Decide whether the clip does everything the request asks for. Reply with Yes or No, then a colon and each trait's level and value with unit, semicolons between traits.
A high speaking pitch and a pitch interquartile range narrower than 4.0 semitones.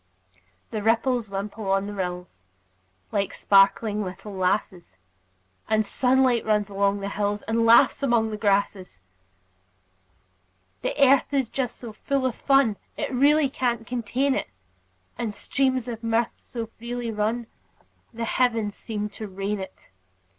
Yes: high, 220 Hz; average, 3.3 semitones